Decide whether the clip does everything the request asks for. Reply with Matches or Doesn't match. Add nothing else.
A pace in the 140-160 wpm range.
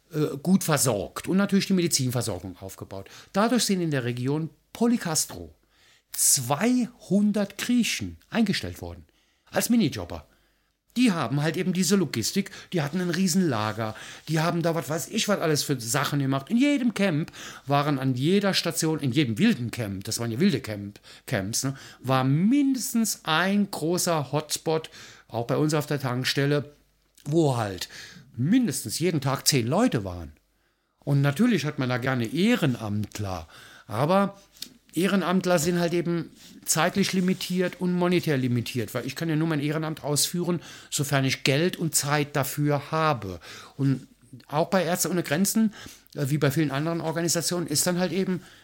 Matches